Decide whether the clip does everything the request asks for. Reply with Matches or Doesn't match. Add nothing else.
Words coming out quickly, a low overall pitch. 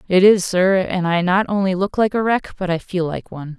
Doesn't match